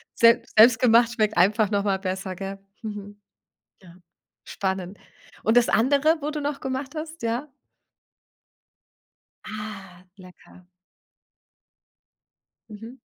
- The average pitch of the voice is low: No, high, 215 Hz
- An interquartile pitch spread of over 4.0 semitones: Yes, average, 4.7 semitones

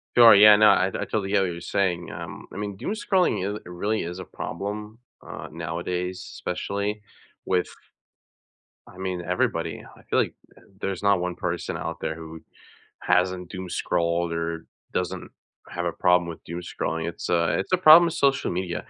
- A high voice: No, very low, 90 Hz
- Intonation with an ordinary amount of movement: Yes, average, 3.0 semitones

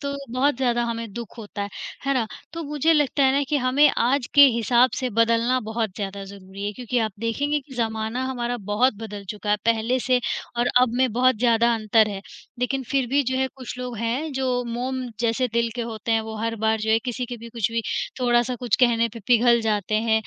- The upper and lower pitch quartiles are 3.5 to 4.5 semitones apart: No, narrow, 2.5 semitones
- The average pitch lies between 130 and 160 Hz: No, high, 235 Hz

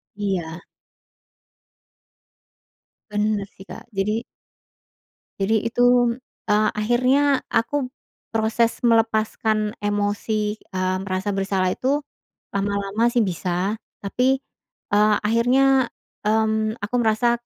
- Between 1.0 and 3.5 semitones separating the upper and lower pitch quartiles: Yes, average, 2.7 semitones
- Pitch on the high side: Yes, high, 215 Hz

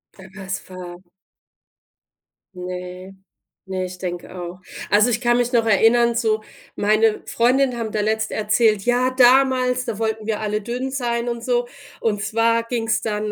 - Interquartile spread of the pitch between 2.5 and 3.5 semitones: Yes, average, 2.9 semitones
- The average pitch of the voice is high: Yes, high, 225 Hz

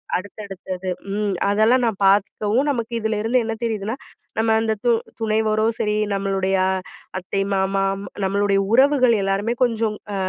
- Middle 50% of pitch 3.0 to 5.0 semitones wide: No, narrow, 2.5 semitones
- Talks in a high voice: Yes, high, 215 Hz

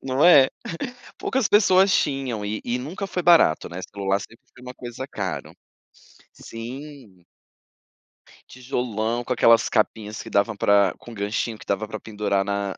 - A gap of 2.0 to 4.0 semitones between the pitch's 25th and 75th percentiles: No, average, 4.6 semitones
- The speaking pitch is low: Yes, low, 115 Hz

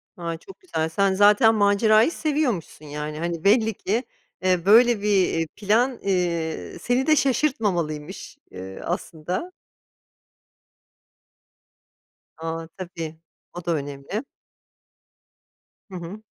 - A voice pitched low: No, high, 190 Hz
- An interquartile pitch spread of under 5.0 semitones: No, average, 5.3 semitones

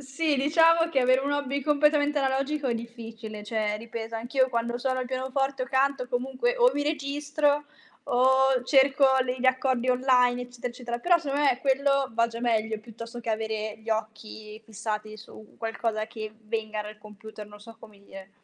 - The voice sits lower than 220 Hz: No, high, 245 Hz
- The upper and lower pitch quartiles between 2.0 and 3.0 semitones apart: No, average, 3.7 semitones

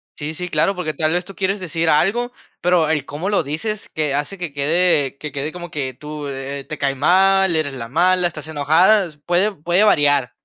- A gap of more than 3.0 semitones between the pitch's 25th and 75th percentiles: Yes, average, 3.9 semitones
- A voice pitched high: No, medium, 160 Hz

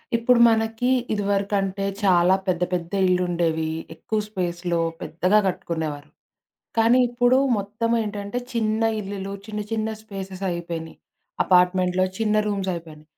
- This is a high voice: Yes, high, 195 Hz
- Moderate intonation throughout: Yes, average, 3.6 semitones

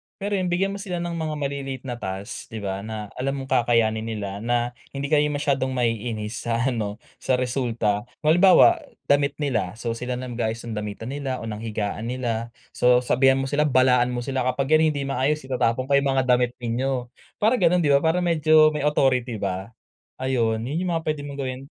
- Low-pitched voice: Yes, low, 130 Hz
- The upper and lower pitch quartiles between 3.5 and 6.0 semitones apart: Yes, average, 3.8 semitones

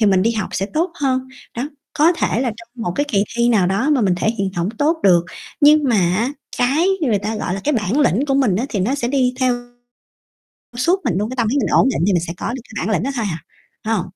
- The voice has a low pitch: No, high, 235 Hz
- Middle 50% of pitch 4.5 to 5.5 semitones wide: Yes, average, 5.0 semitones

